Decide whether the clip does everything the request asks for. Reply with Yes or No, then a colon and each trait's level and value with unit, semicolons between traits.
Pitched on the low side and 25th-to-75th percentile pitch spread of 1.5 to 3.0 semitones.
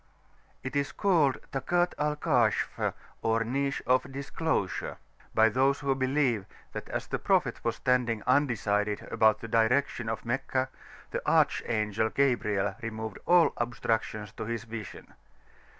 No: low, 120 Hz; average, 3.8 semitones